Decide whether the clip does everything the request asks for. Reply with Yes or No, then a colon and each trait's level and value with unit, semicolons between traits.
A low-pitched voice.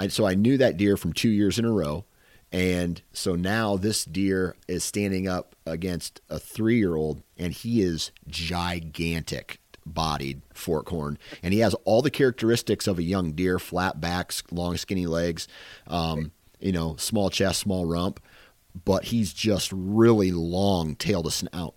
Yes: very low, 90 Hz